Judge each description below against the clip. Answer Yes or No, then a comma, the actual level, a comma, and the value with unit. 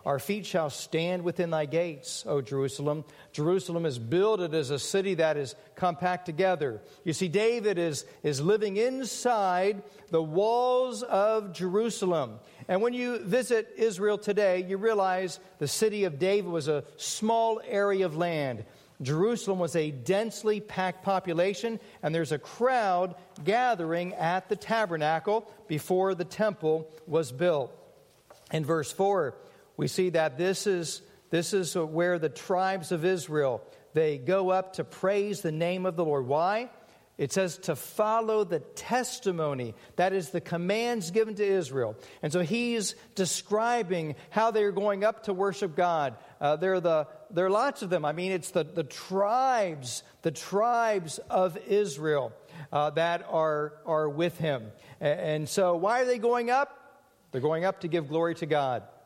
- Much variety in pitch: No, average, 4.5 semitones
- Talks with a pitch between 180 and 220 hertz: Yes, medium, 185 Hz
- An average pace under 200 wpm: Yes, average, 160 wpm